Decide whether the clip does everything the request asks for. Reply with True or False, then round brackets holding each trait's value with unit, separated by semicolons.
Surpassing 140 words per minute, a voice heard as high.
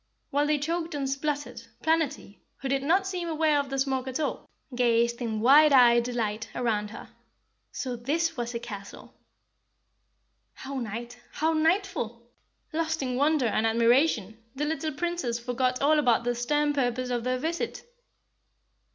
True (155 wpm; 265 Hz)